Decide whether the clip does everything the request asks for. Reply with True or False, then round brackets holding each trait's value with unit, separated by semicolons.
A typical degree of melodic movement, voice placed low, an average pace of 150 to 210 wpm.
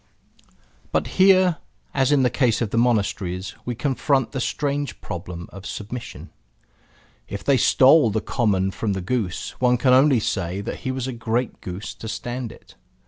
True (4.7 semitones; 120 Hz; 170 wpm)